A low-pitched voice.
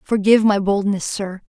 No: high, 200 Hz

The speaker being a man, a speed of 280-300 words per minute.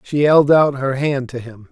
No: male; fast, 245 wpm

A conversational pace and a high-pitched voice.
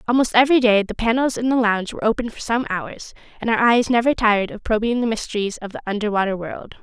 No: fast, 230 wpm; high, 225 Hz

